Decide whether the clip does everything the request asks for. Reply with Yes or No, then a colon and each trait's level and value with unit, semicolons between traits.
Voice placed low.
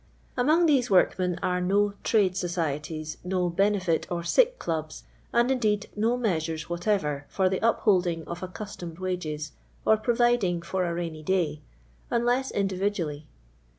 No: medium, 185 Hz